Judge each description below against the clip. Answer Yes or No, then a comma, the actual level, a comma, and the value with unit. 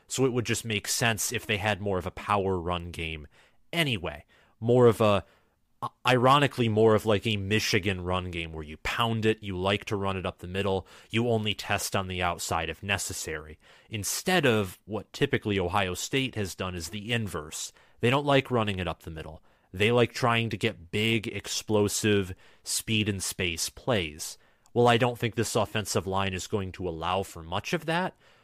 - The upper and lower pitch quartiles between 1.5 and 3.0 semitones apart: No, average, 4.0 semitones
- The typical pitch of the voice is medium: No, low, 105 Hz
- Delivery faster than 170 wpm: Yes, average, 195 wpm